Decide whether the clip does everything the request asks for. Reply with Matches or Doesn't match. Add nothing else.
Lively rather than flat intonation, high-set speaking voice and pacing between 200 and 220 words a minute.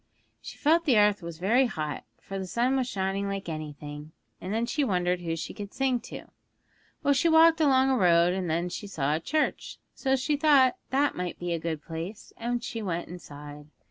Matches